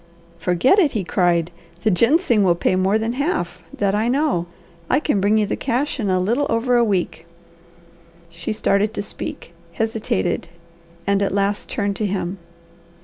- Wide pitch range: No, average, 4.2 semitones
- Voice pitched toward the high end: Yes, high, 205 Hz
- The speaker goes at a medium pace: Yes, average, 170 wpm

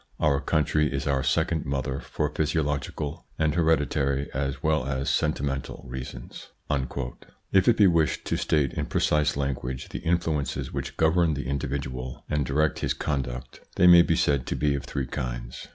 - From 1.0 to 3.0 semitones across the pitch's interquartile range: Yes, narrow, 2.6 semitones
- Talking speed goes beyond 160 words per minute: Yes, average, 170 wpm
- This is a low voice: Yes, very low, 70 Hz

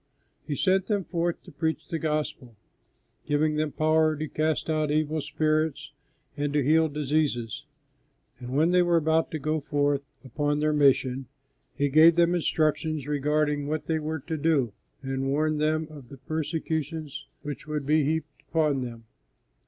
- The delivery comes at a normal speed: Yes, average, 160 wpm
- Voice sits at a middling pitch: Yes, medium, 155 Hz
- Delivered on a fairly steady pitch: Yes, narrow, 1.7 semitones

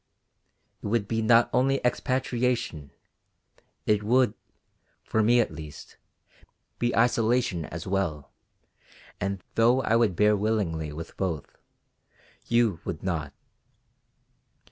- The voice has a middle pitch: No, low, 105 Hz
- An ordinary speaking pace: No, slow, 110 wpm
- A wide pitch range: Yes, wide, 6.0 semitones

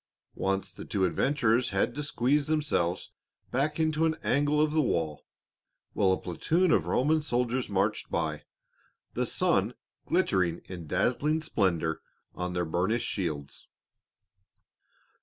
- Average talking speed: No, slow, 130 wpm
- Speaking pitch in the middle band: No, low, 115 Hz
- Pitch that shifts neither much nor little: No, wide, 8.8 semitones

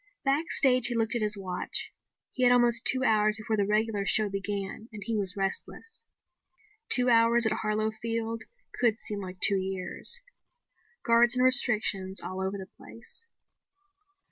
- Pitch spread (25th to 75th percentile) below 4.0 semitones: Yes, average, 3.0 semitones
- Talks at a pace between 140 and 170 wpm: Yes, average, 155 wpm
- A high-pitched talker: Yes, high, 220 Hz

